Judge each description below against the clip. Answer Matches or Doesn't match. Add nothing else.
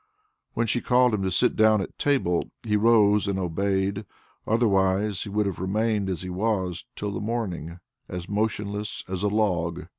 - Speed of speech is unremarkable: Matches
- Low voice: Matches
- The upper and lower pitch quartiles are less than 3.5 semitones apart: Matches